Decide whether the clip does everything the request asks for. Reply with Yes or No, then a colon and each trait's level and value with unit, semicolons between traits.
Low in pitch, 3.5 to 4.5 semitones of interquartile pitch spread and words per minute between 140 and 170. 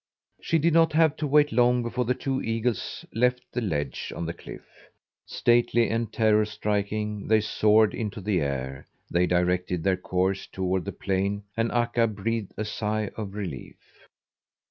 Yes: low, 105 Hz; average, 3.9 semitones; average, 165 wpm